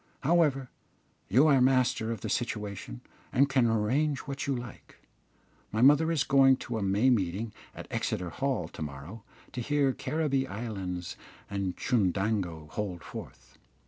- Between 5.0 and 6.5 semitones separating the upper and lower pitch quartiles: Yes, wide, 5.6 semitones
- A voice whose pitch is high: No, low, 115 Hz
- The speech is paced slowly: No, average, 145 wpm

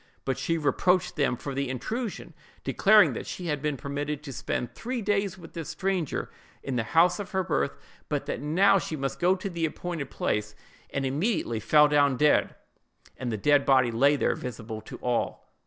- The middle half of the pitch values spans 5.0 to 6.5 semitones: Yes, wide, 5.4 semitones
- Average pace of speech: Yes, average, 190 wpm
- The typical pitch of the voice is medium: Yes, medium, 150 Hz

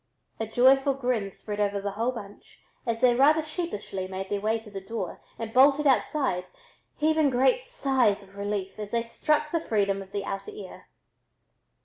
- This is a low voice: No, high, 230 Hz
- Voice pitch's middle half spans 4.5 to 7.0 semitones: Yes, average, 5.3 semitones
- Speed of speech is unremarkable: Yes, average, 175 wpm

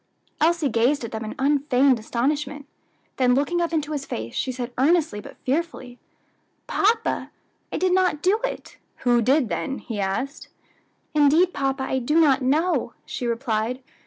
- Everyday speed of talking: Yes, average, 160 wpm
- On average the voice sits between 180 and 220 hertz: No, very high, 275 Hz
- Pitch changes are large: No, average, 4.1 semitones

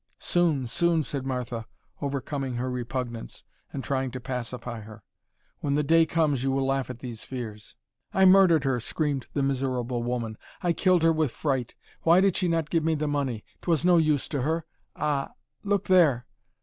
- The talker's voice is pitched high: No, medium, 140 Hz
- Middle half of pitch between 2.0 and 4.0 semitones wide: No, average, 4.5 semitones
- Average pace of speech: Yes, average, 180 wpm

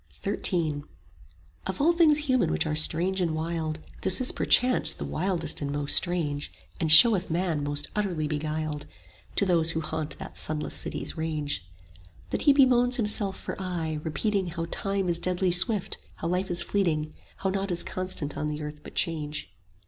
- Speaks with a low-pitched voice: No, medium, 170 Hz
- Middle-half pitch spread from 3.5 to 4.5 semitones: Yes, average, 3.9 semitones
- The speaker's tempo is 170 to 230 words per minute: Yes, average, 175 wpm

